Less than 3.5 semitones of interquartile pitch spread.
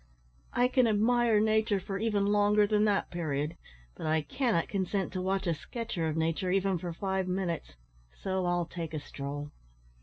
No: average, 4.0 semitones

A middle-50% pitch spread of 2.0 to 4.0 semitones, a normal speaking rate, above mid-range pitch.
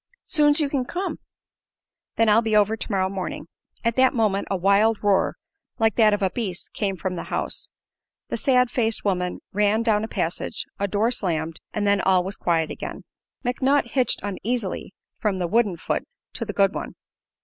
Yes: average, 3.4 semitones; average, 180 wpm; high, 210 Hz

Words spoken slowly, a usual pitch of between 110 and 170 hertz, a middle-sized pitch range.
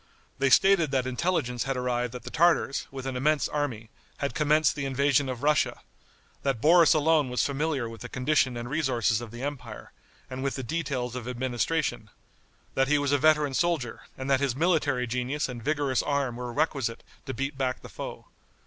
No: average, 190 wpm; low, 135 Hz; average, 3.1 semitones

